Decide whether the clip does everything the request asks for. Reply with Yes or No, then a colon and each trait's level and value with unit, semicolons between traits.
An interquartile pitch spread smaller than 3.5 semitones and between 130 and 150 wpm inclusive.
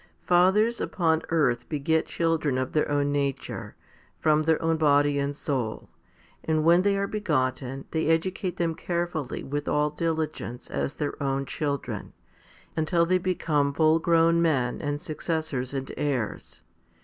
Yes: average, 2.8 semitones; average, 145 wpm